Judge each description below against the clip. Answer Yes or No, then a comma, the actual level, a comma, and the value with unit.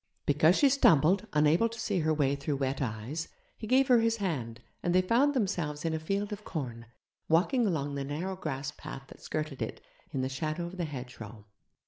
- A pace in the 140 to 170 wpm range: No, average, 200 wpm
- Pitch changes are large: Yes, wide, 6.1 semitones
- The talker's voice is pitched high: No, medium, 155 Hz